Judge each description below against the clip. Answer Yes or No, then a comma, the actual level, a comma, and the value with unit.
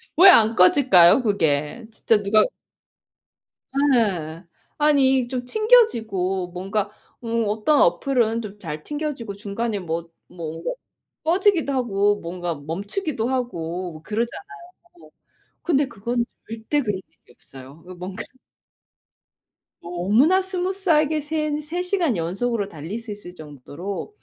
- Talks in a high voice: Yes, high, 220 Hz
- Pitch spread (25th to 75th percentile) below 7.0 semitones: No, wide, 8.1 semitones